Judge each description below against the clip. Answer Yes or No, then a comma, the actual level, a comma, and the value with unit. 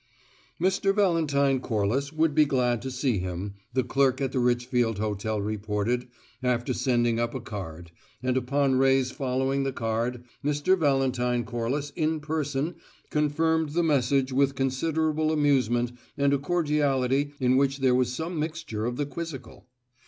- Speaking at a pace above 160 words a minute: No, average, 150 wpm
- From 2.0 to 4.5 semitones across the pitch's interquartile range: Yes, average, 3.3 semitones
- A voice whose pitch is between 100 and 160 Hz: Yes, low, 135 Hz